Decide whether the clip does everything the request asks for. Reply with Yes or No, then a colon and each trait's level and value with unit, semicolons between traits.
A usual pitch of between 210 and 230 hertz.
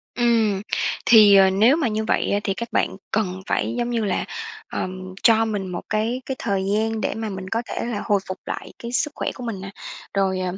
Yes: high, 215 Hz